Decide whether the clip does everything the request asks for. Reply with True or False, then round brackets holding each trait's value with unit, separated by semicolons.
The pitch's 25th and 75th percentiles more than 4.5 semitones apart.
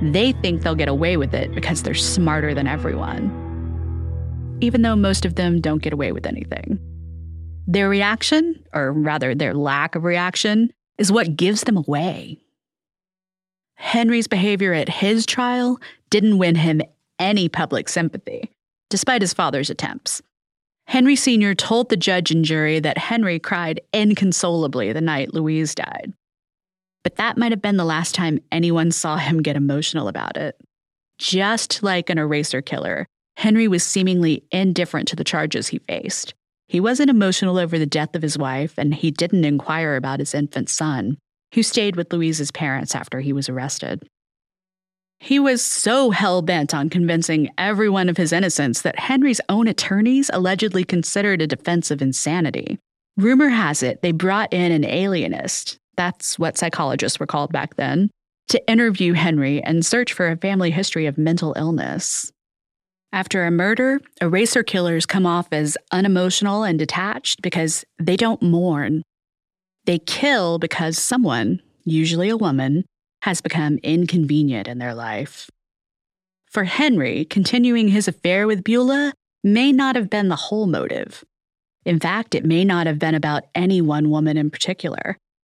True (4.9 semitones)